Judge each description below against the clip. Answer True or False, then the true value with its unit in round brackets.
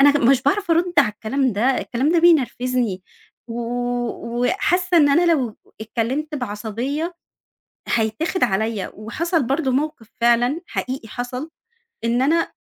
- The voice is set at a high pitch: True (260 Hz)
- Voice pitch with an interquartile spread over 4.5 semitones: True (5.2 semitones)